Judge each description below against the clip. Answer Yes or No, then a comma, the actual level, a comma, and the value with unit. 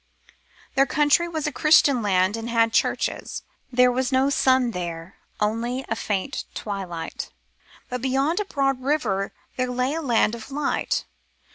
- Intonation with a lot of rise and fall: No, average, 4.2 semitones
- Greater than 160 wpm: No, average, 150 wpm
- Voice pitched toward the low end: No, very high, 250 Hz